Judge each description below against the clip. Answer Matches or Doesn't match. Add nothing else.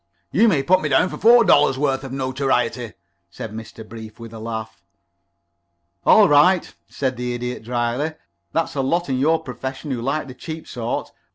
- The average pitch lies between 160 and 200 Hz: Doesn't match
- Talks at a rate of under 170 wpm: Doesn't match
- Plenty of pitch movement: Doesn't match